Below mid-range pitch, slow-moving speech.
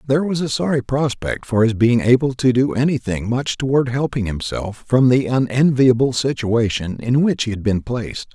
No: low, 125 Hz; average, 185 wpm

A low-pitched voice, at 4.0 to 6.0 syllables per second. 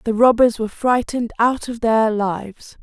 No: high, 230 Hz; 4.9 syllables/s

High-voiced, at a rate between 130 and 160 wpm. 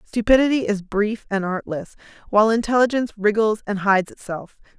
Yes: high, 215 Hz; average, 140 wpm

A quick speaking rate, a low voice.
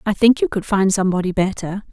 No: fast, 220 wpm; high, 200 Hz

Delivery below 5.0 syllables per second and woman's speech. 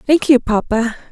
Yes: 4.7 syllables/s; female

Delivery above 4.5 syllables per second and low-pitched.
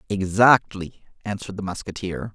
Yes: 5.0 syllables/s; low, 100 Hz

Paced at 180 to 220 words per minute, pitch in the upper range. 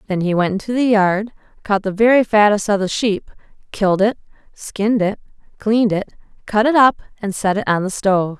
Yes: average, 200 wpm; high, 205 Hz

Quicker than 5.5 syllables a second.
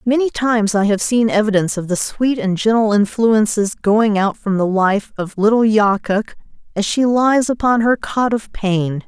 No: 4.7 syllables/s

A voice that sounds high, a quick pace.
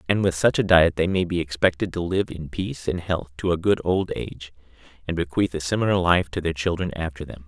No: very low, 85 Hz; fast, 240 wpm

